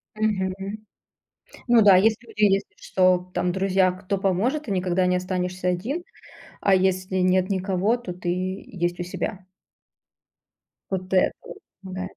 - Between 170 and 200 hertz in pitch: Yes, medium, 185 Hz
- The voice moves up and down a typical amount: No, narrow, 1.5 semitones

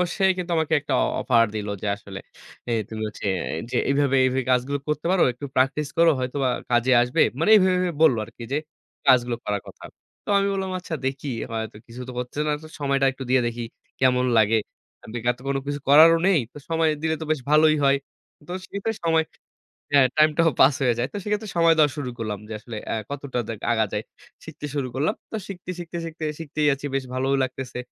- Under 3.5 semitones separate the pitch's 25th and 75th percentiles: No, average, 4.3 semitones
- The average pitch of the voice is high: No, medium, 140 Hz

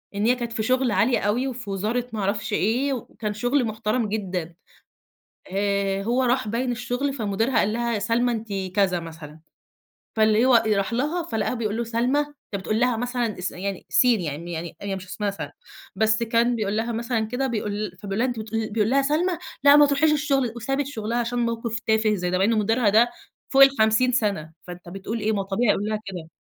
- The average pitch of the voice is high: Yes, high, 225 Hz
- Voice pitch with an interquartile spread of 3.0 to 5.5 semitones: Yes, average, 3.3 semitones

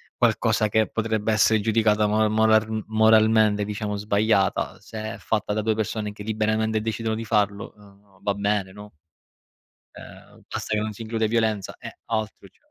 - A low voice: Yes, low, 110 Hz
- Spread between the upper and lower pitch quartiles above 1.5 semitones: No, narrow, 1.0 semitones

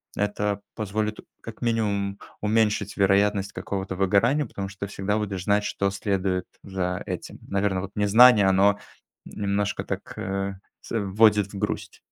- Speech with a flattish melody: Yes, narrow, 1.3 semitones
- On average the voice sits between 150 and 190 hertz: No, low, 100 Hz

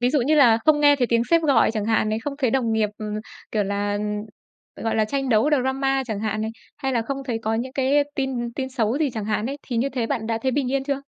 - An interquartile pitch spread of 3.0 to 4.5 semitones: Yes, average, 3.7 semitones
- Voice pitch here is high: Yes, high, 245 Hz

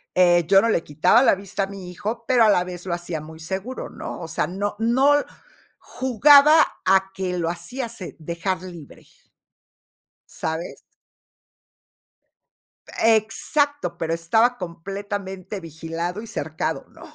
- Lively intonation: No, average, 4.9 semitones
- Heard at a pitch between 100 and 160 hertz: No, high, 190 Hz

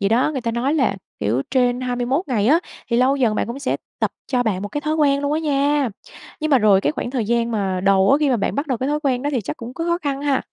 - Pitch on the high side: Yes, very high, 255 Hz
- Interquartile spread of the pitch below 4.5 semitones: Yes, average, 3.8 semitones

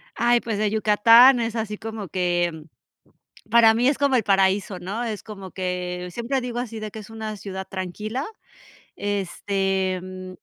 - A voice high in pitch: Yes, high, 210 Hz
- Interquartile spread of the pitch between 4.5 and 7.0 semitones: No, average, 3.3 semitones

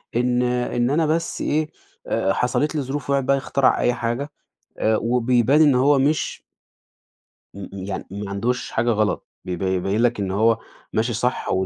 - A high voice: No, low, 120 Hz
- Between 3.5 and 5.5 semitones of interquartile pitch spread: Yes, average, 4.2 semitones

